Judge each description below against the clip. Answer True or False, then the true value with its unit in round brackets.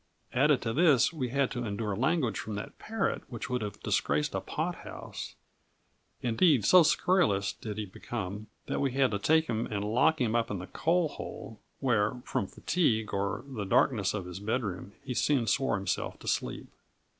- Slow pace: False (185 wpm)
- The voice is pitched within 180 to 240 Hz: False (115 Hz)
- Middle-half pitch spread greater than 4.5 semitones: True (5.0 semitones)